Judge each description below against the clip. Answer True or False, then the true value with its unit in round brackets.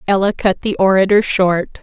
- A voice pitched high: True (195 Hz)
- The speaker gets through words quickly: False (165 wpm)